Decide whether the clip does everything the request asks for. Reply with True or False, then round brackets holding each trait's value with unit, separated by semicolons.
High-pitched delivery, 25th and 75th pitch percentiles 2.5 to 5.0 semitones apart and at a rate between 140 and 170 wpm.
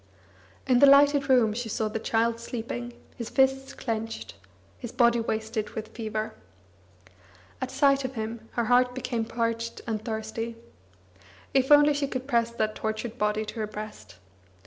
True (235 Hz; 2.8 semitones; 155 wpm)